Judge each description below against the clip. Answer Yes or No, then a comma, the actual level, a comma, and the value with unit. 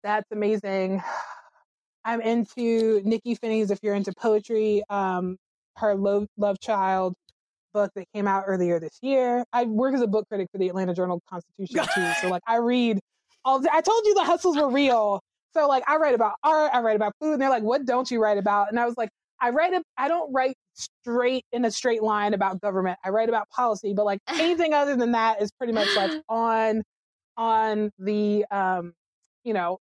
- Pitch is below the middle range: No, high, 220 Hz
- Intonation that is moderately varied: Yes, average, 3.8 semitones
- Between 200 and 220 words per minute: Yes, fast, 205 wpm